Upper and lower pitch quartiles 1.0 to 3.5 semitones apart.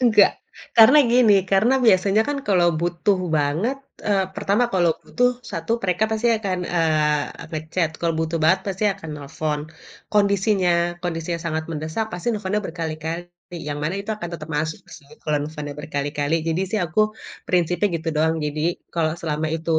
No: average, 4.2 semitones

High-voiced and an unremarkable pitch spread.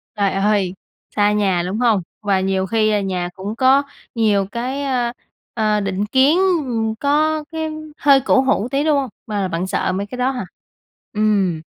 Yes: high, 215 Hz; average, 5.0 semitones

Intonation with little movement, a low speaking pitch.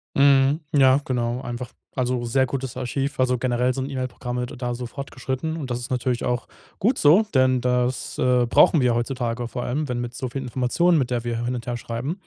Yes: narrow, 1.7 semitones; low, 125 Hz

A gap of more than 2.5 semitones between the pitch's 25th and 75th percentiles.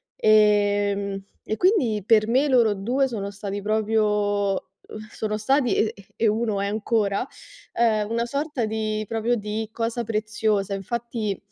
No: narrow, 2.1 semitones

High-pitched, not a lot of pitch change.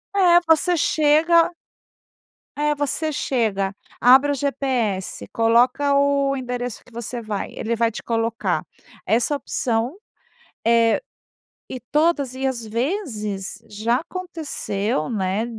No: very high, 250 Hz; average, 4.3 semitones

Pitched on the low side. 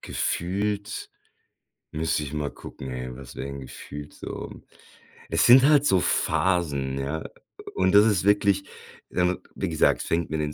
Yes: very low, 85 Hz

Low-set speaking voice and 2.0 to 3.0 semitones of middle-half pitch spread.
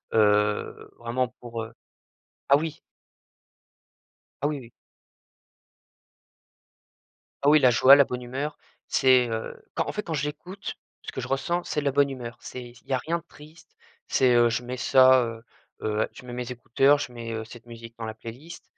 No: low, 125 Hz; average, 3.5 semitones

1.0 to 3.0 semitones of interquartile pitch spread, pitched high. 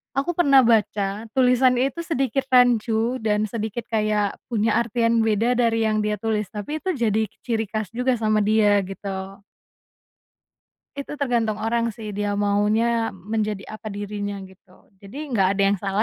Yes: narrow, 2.5 semitones; high, 220 Hz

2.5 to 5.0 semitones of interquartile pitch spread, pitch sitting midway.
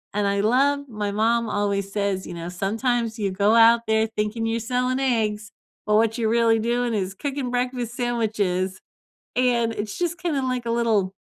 No: average, 3.0 semitones; high, 225 Hz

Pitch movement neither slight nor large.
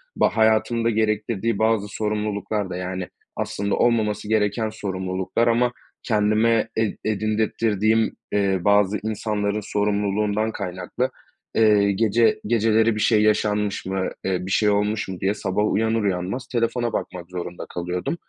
No: narrow, 2.0 semitones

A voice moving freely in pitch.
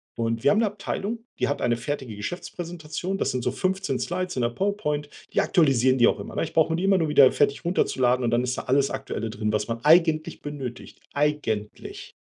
Yes: wide, 6.0 semitones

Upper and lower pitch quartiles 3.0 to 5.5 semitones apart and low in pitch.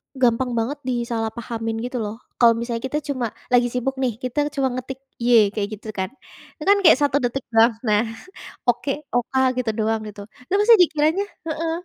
No: average, 3.5 semitones; high, 245 Hz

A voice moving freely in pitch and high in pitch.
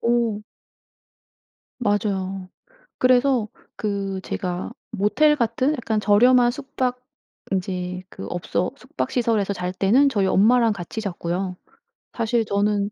No: average, 4.2 semitones; high, 210 Hz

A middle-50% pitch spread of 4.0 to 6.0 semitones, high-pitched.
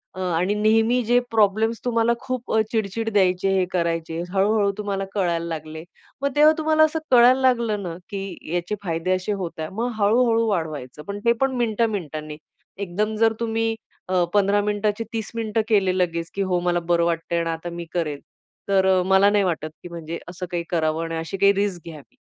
Yes: average, 4.6 semitones; high, 195 Hz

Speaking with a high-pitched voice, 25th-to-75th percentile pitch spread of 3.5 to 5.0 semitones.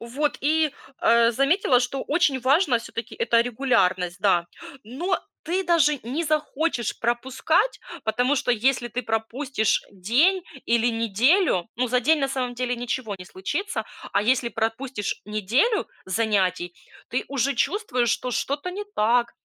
Yes: high, 245 Hz; average, 4.3 semitones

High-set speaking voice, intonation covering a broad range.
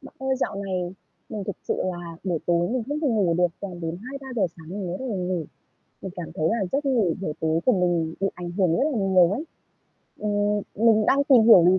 No: high, 195 Hz; average, 4.7 semitones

